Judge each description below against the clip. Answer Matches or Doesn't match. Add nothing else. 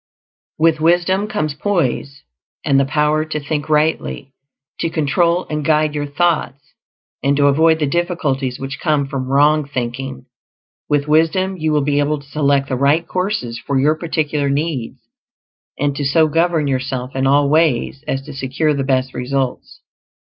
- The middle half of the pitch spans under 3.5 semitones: Matches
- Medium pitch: Matches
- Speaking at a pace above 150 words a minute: Matches